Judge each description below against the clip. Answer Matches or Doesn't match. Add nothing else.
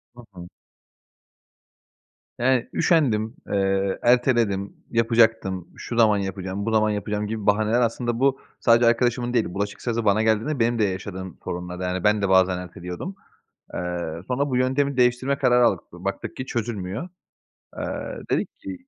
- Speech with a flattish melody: Doesn't match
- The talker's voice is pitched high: Doesn't match